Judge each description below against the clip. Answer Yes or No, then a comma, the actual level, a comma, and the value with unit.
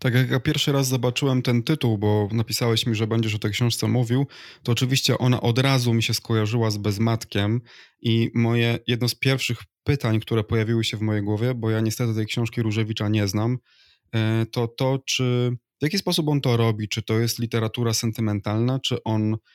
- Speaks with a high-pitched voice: No, low, 115 Hz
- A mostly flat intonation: Yes, narrow, 2.1 semitones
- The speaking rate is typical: No, fast, 195 wpm